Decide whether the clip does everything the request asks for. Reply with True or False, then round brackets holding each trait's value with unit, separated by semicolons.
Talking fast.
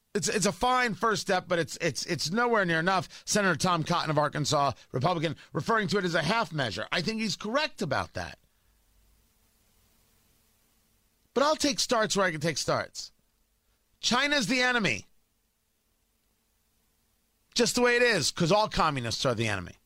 False (165 wpm)